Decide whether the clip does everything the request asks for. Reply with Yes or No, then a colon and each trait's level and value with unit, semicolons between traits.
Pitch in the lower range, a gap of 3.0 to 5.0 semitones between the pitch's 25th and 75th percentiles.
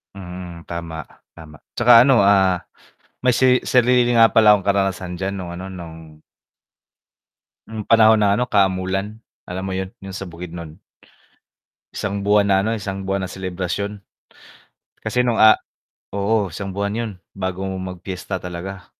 No: very low, 95 Hz; narrow, 2.4 semitones